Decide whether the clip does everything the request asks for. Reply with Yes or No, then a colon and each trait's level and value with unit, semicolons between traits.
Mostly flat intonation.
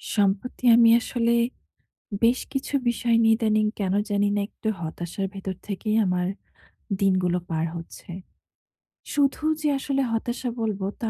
No: average, 3.7 semitones